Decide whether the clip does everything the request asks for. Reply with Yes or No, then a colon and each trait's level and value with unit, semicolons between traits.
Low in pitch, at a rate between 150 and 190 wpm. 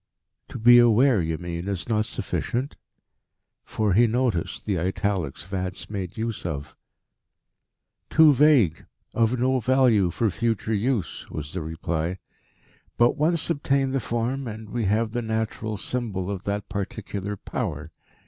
No: low, 110 Hz; average, 140 wpm